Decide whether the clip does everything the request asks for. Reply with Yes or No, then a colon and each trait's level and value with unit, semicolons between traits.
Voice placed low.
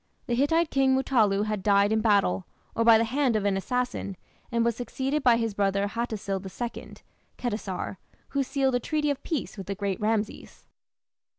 No: high, 230 Hz